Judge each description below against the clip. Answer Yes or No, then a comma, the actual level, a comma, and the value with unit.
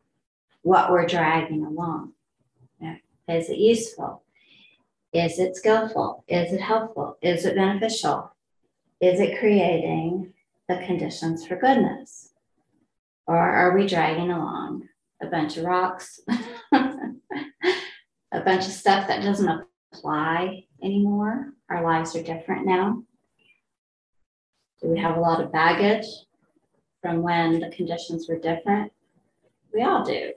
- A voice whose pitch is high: No, medium, 180 Hz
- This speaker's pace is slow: Yes, slow, 125 wpm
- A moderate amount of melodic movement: Yes, average, 4.5 semitones